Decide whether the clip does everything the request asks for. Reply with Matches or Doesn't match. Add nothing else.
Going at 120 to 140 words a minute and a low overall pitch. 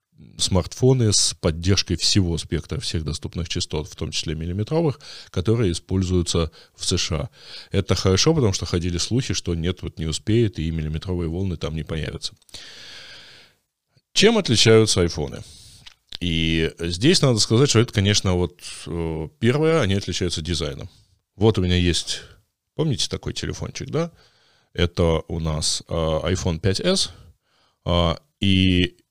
Matches